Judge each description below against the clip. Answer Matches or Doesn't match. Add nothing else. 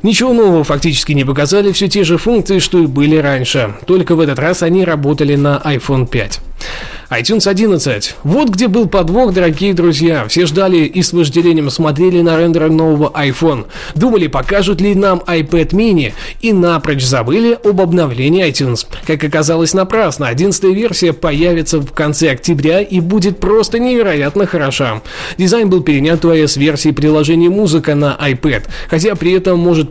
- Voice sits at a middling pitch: Matches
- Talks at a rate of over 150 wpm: Matches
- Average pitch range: Matches